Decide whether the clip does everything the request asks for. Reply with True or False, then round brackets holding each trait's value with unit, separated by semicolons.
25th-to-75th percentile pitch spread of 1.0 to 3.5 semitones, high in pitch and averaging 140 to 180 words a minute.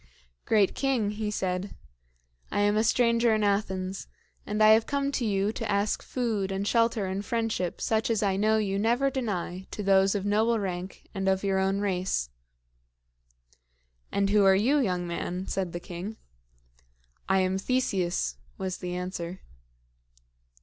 True (2.6 semitones; 200 Hz; 160 wpm)